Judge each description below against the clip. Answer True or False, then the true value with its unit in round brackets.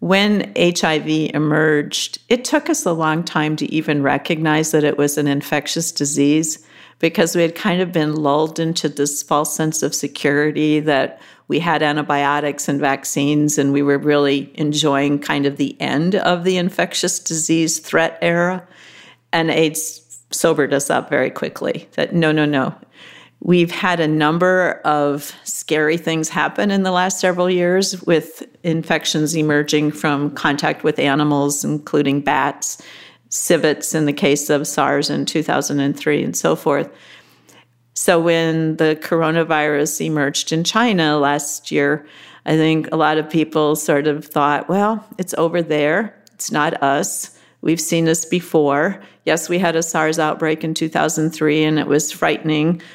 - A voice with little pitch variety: True (2.1 semitones)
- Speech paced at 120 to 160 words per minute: True (155 wpm)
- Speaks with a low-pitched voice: False (155 Hz)